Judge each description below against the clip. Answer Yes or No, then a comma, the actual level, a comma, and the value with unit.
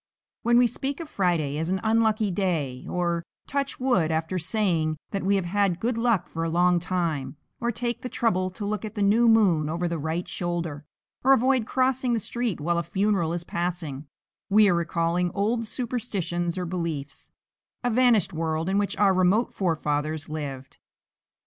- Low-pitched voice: No, medium, 185 Hz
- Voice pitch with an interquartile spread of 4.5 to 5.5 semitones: Yes, average, 5.0 semitones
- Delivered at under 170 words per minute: No, average, 180 wpm